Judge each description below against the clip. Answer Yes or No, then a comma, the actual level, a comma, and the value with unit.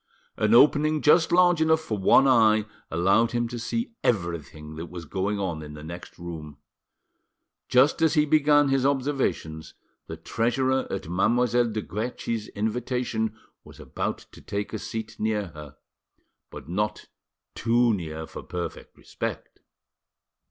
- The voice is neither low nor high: No, low, 110 Hz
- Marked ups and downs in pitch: Yes, wide, 7.0 semitones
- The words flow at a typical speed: Yes, average, 145 wpm